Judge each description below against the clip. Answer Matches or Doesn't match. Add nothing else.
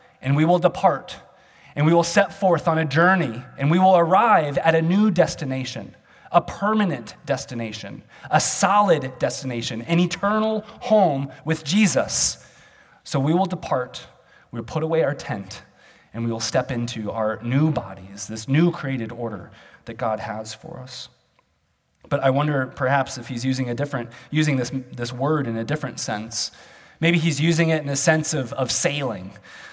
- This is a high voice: Doesn't match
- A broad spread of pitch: Matches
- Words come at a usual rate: Matches